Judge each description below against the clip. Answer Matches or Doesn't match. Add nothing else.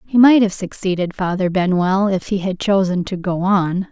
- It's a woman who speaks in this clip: Matches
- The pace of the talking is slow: Doesn't match